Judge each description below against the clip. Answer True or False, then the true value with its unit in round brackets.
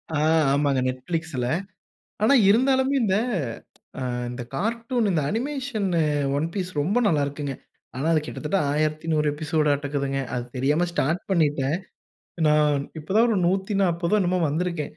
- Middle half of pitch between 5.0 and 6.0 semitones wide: True (5.4 semitones)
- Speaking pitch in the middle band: True (165 Hz)